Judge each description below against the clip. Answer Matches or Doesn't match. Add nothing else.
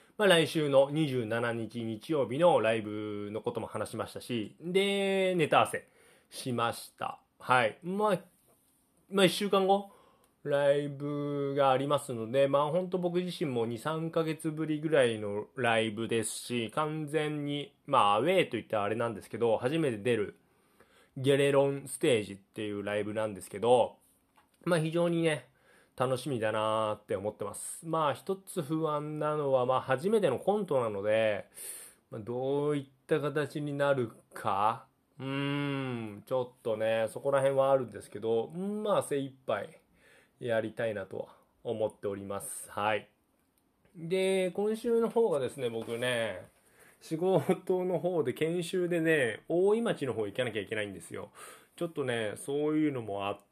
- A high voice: Doesn't match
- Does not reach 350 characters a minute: Matches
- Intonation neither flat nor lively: Doesn't match